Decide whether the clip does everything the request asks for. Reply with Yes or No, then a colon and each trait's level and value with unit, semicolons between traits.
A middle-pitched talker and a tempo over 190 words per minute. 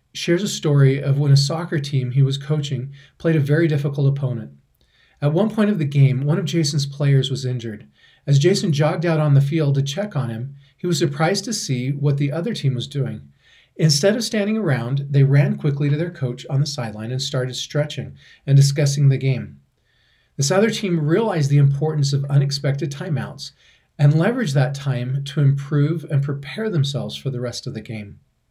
Yes: medium, 145 Hz; average, 200 wpm